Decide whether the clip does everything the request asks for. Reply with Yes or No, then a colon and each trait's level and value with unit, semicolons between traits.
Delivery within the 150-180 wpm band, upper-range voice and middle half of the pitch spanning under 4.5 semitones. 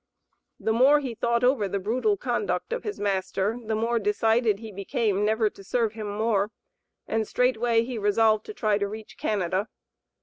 Yes: average, 175 wpm; high, 220 Hz; narrow, 2.4 semitones